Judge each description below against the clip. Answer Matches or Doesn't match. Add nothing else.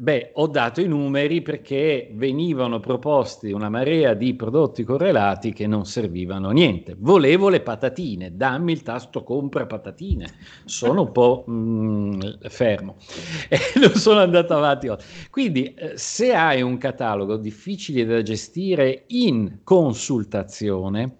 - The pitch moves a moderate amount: Doesn't match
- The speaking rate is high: Doesn't match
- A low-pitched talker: Matches